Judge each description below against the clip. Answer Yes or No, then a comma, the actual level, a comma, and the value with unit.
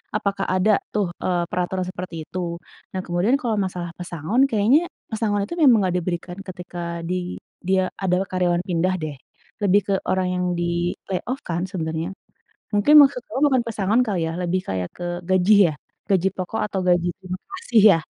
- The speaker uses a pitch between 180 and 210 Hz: Yes, medium, 185 Hz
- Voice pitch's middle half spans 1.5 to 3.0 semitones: Yes, average, 2.7 semitones